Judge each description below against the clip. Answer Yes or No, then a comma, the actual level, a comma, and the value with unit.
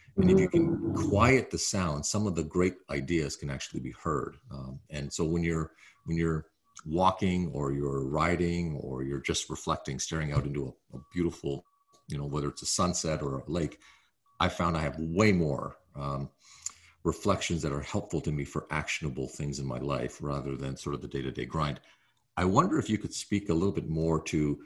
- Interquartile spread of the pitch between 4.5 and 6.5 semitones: No, average, 3.5 semitones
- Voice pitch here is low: Yes, very low, 80 Hz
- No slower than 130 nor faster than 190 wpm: No, average, 200 wpm